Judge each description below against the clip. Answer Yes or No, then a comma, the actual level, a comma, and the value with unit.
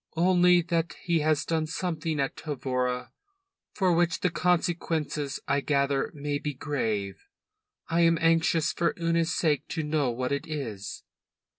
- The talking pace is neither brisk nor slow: Yes, average, 145 wpm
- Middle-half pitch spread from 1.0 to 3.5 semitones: Yes, average, 3.0 semitones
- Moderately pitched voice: Yes, medium, 155 Hz